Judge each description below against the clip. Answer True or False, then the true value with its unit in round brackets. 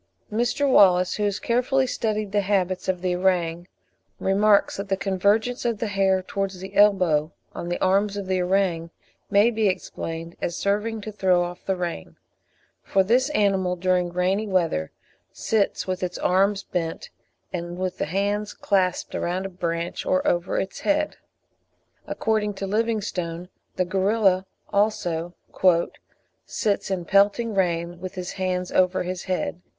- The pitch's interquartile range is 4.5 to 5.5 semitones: False (2.4 semitones)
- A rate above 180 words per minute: False (155 wpm)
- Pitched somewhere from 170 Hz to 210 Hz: True (190 Hz)